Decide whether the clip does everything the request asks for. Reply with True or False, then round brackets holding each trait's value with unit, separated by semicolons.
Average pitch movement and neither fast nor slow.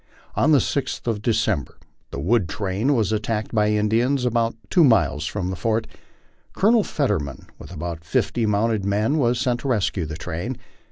True (4.5 semitones; 170 wpm)